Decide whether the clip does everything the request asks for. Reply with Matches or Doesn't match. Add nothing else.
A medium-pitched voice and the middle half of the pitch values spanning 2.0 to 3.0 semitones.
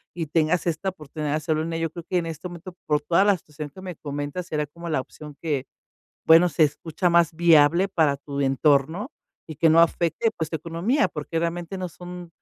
Matches